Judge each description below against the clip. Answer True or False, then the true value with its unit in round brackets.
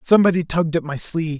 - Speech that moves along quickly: True (215 wpm)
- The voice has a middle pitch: True (165 Hz)